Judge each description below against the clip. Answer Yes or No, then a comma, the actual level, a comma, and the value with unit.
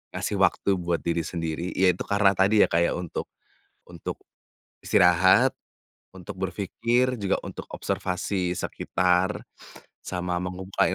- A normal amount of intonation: No, narrow, 1.8 semitones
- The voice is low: Yes, very low, 90 Hz